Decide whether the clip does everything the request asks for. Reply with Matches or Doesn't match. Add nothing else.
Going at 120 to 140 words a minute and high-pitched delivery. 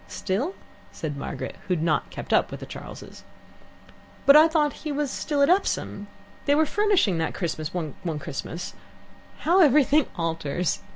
Doesn't match